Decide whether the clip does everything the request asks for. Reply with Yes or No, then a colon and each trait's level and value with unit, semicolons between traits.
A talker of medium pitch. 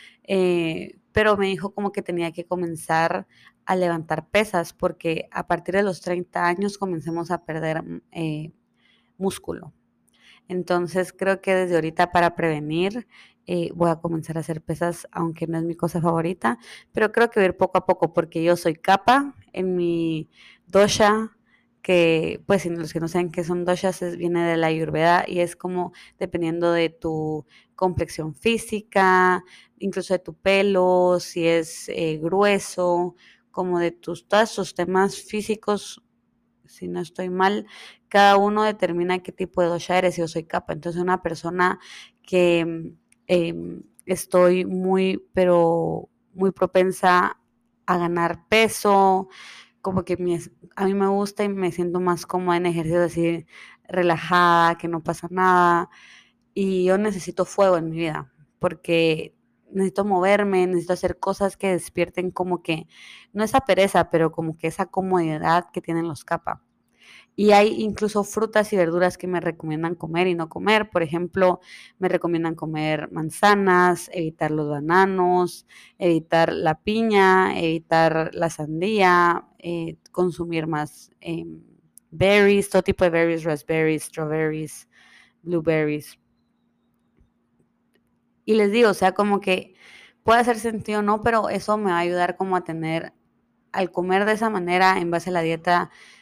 Yes: medium, 180 Hz